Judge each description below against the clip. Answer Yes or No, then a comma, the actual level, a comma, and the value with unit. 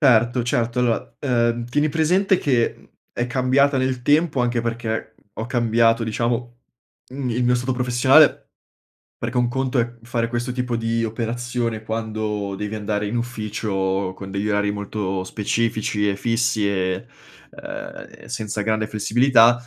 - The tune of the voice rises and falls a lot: No, narrow, 2.4 semitones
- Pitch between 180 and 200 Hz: No, low, 115 Hz